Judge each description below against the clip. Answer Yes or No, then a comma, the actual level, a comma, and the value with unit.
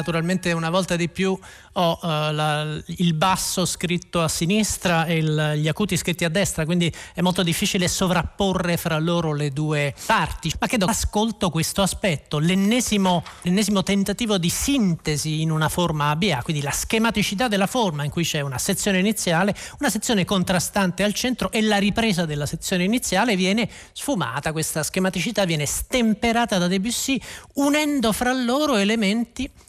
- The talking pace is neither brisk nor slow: Yes, average, 160 wpm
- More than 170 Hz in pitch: Yes, medium, 185 Hz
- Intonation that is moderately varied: Yes, average, 4.0 semitones